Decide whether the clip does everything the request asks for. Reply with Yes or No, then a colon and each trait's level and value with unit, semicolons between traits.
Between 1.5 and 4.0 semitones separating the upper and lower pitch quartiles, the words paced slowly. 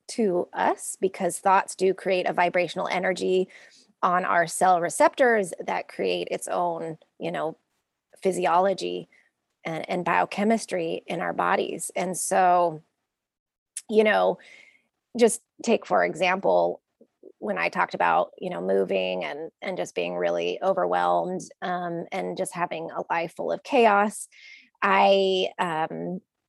Yes: average, 2.8 semitones; slow, 130 wpm